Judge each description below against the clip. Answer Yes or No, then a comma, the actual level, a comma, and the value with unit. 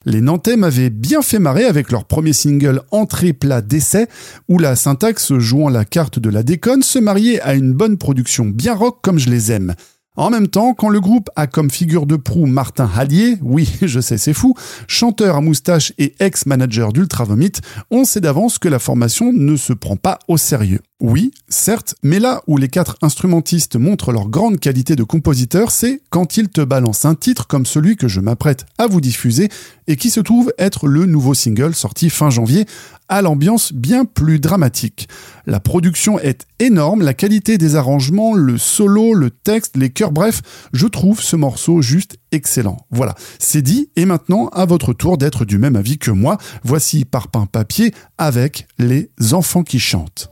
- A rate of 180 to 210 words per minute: Yes, average, 190 wpm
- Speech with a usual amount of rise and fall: No, wide, 7.5 semitones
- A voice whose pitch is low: No, medium, 155 Hz